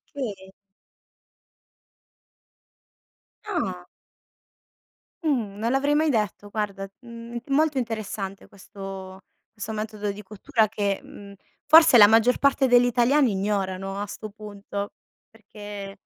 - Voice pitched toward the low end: No, high, 210 Hz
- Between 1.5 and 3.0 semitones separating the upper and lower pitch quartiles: No, average, 3.6 semitones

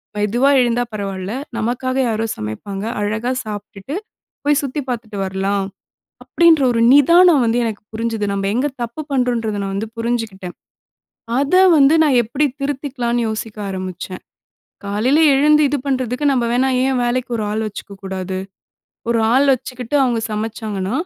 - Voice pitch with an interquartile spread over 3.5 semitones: Yes, average, 4.2 semitones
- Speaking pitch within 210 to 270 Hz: Yes, high, 235 Hz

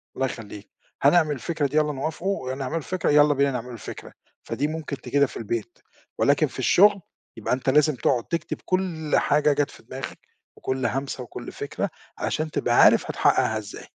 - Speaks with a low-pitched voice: No, medium, 145 Hz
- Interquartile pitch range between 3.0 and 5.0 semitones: Yes, average, 3.4 semitones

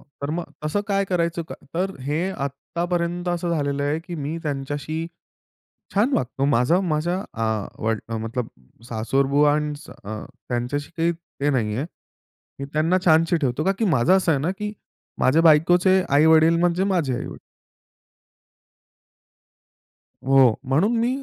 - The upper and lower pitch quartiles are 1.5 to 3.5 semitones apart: No, average, 4.1 semitones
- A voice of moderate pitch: Yes, medium, 155 Hz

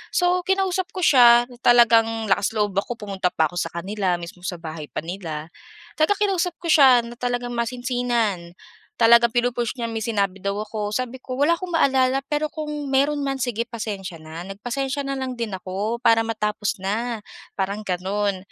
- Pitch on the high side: Yes, high, 230 Hz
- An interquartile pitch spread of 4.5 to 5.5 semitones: Yes, average, 4.8 semitones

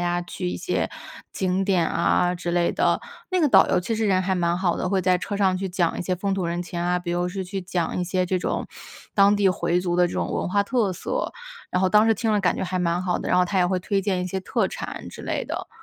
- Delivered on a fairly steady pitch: Yes, narrow, 1.7 semitones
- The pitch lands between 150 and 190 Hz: Yes, medium, 185 Hz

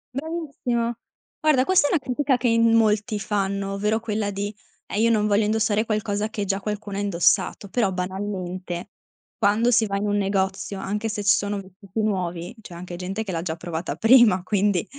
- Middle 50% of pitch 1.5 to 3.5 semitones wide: Yes, narrow, 2.5 semitones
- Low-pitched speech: No, high, 205 Hz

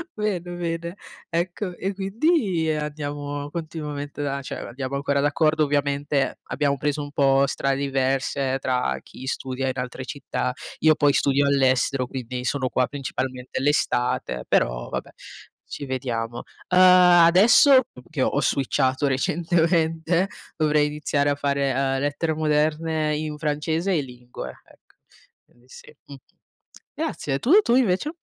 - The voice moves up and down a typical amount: Yes, average, 3.3 semitones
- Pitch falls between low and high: Yes, medium, 145 Hz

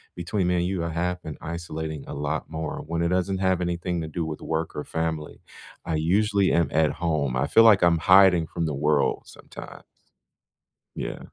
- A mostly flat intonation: Yes, narrow, 2.2 semitones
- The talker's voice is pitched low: Yes, very low, 85 Hz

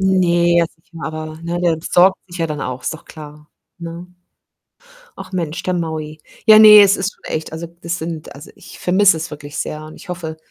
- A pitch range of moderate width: No, narrow, 2.3 semitones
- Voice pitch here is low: No, medium, 170 Hz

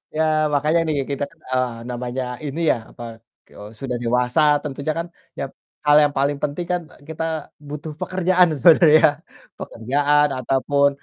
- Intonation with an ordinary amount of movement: Yes, average, 3.5 semitones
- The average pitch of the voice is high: No, medium, 145 Hz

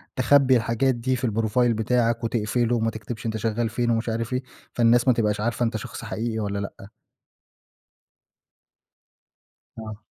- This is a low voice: Yes, low, 115 Hz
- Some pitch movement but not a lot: No, narrow, 1.7 semitones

